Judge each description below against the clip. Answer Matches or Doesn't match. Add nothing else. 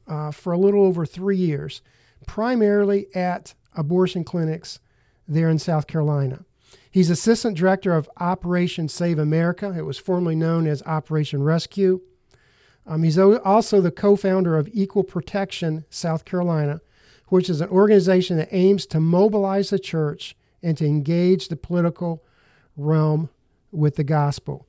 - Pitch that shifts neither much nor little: Matches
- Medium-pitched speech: Matches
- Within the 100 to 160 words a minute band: Matches